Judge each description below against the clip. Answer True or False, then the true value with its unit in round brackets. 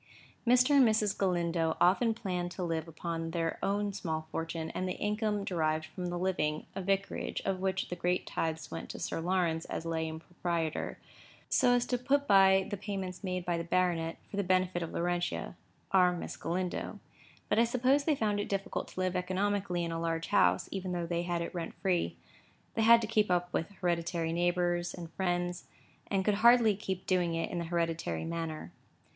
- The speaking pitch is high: False (180 Hz)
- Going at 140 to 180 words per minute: False (190 wpm)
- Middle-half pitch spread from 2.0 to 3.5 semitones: True (2.9 semitones)